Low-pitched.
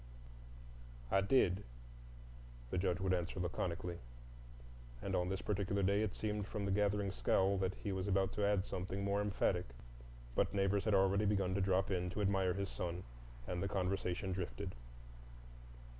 Yes: very low, 95 Hz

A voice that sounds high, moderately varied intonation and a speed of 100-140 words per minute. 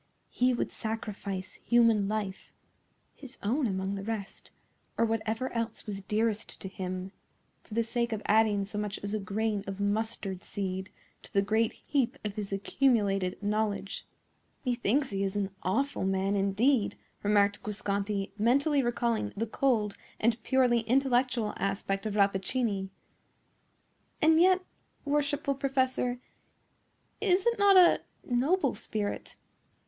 Yes: high, 220 Hz; average, 4.0 semitones; slow, 135 wpm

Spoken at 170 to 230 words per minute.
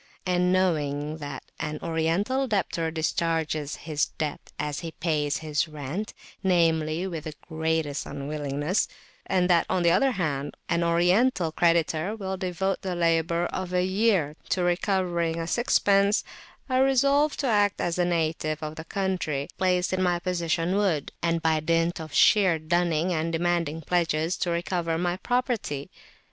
No: average, 155 wpm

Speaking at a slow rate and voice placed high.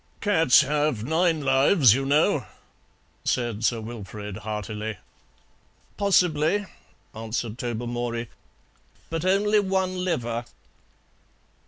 No: slow, 85 wpm; low, 135 Hz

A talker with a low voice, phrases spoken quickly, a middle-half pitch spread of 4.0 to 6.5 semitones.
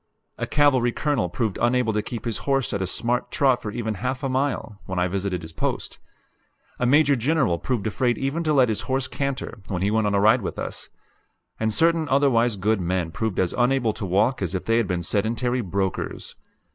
Yes: low, 115 Hz; fast, 210 wpm; average, 4.7 semitones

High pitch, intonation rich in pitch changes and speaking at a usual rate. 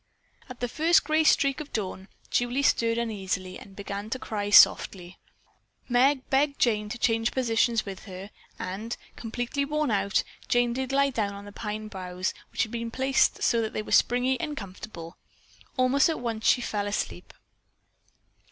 No: high, 230 Hz; average, 4.2 semitones; average, 170 wpm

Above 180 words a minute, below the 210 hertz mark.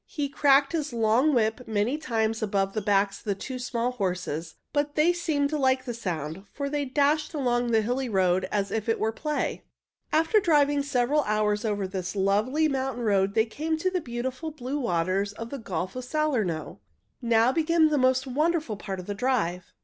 No: average, 195 wpm; high, 245 Hz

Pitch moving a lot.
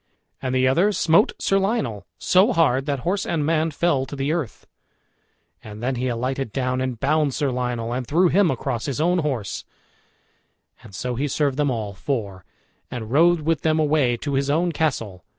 No: average, 4.4 semitones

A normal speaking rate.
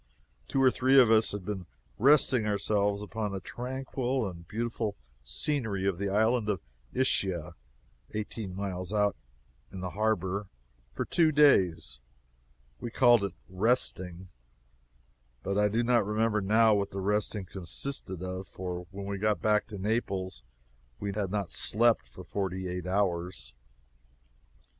Yes: average, 145 wpm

